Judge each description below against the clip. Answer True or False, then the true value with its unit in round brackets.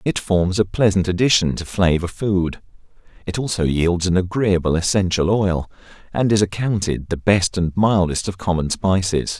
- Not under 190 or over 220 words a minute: False (160 wpm)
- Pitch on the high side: False (95 Hz)